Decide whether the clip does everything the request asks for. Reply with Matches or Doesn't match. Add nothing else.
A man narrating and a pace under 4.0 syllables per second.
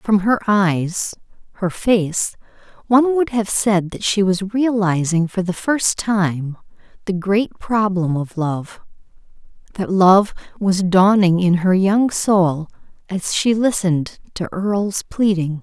Doesn't match